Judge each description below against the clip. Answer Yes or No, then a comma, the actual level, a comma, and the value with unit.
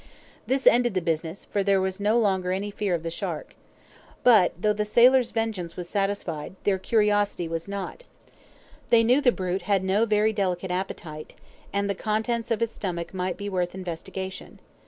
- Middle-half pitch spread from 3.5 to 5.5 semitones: No, average, 3.1 semitones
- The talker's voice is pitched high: Yes, high, 200 Hz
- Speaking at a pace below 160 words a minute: No, average, 180 wpm